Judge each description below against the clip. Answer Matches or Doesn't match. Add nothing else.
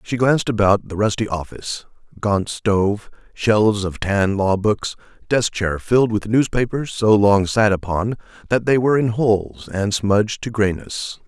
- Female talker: Doesn't match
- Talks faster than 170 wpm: Doesn't match